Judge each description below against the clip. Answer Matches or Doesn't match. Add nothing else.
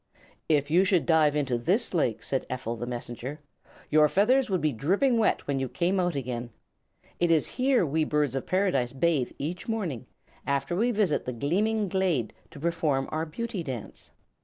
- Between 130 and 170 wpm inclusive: Doesn't match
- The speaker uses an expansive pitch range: Matches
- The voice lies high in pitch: Doesn't match